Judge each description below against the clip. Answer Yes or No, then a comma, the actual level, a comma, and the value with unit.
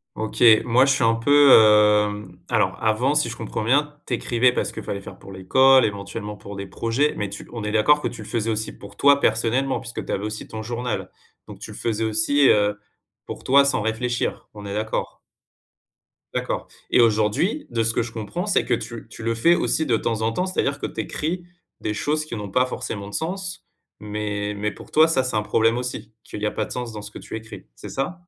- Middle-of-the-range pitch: No, low, 115 Hz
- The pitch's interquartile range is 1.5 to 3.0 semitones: No, average, 3.8 semitones